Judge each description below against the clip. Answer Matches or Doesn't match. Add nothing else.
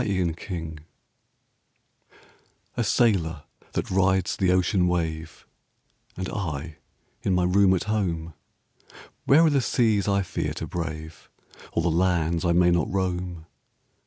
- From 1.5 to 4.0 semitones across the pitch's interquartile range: Matches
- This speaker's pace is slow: Matches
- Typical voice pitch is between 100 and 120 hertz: Doesn't match